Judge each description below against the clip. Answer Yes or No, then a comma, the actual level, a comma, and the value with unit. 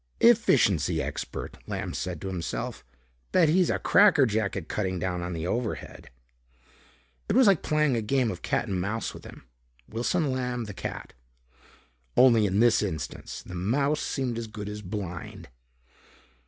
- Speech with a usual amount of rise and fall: No, wide, 6.1 semitones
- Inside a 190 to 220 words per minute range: No, average, 160 wpm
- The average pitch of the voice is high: No, low, 110 Hz